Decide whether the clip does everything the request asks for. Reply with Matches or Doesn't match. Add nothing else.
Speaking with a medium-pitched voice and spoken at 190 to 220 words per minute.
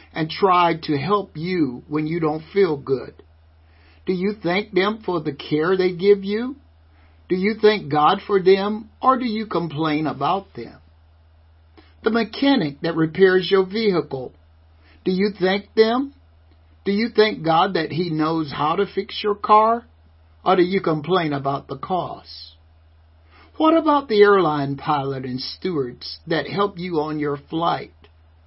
Doesn't match